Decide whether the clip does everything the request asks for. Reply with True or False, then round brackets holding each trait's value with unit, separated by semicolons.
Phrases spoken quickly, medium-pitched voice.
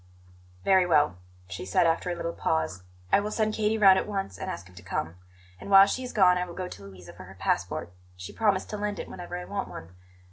True (245 wpm; 180 Hz)